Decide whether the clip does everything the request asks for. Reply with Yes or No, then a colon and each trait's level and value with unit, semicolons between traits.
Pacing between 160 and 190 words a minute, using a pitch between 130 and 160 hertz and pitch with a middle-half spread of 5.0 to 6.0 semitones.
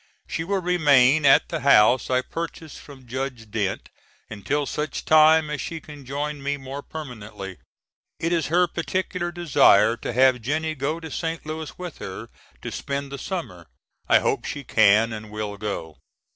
Yes: average, 170 wpm; medium, 140 Hz; average, 5.3 semitones